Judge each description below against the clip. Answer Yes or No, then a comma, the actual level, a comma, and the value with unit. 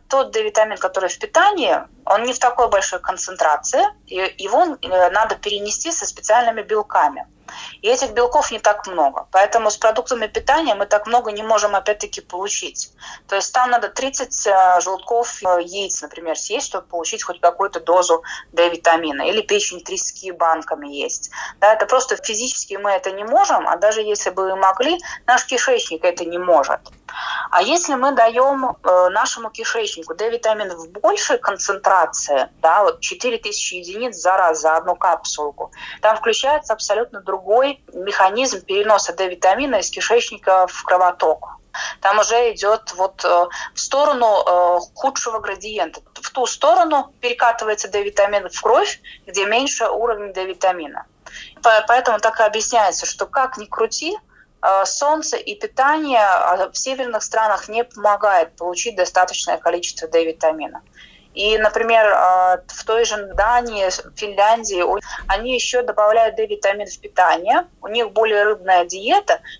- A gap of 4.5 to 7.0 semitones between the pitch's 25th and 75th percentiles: Yes, average, 5.0 semitones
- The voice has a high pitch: Yes, high, 215 Hz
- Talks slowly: No, average, 140 wpm